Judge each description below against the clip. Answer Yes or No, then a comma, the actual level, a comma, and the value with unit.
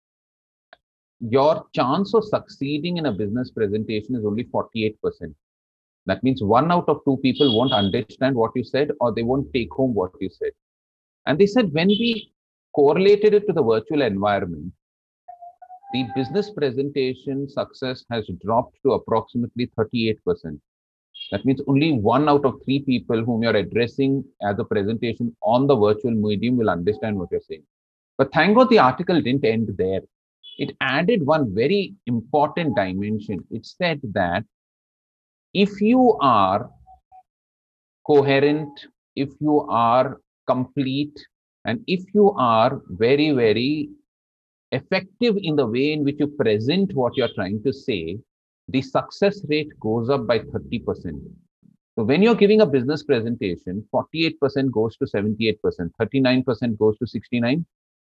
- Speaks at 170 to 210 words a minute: No, average, 145 wpm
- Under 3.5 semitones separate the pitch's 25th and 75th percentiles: No, wide, 5.5 semitones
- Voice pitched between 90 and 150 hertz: Yes, low, 135 Hz